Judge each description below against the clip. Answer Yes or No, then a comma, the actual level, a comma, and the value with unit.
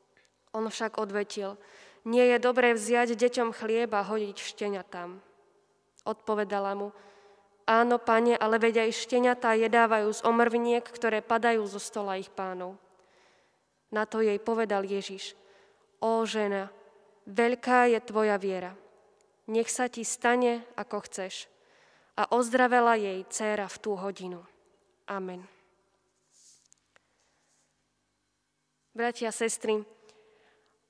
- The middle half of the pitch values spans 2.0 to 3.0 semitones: Yes, narrow, 2.4 semitones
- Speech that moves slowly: Yes, slow, 105 wpm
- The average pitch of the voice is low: No, high, 215 Hz